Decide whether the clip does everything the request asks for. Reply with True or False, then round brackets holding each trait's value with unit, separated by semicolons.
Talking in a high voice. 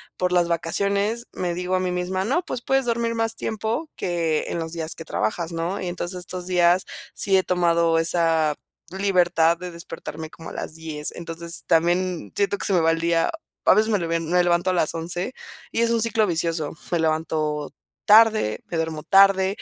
False (175 Hz)